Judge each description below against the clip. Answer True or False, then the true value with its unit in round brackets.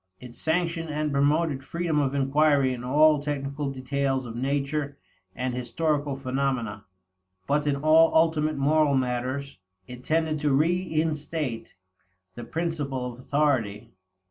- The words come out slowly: True (125 wpm)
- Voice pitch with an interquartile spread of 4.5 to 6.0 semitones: False (2.9 semitones)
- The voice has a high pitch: False (140 Hz)